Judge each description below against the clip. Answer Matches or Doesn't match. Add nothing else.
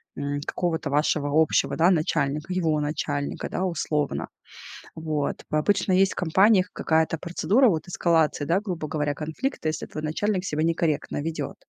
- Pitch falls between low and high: Matches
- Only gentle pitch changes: Doesn't match